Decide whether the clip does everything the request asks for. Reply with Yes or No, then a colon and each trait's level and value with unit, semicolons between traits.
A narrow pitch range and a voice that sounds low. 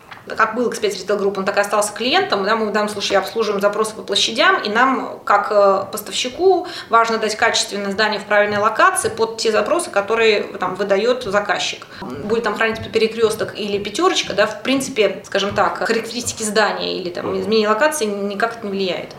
No: narrow, 2.2 semitones; high, 215 Hz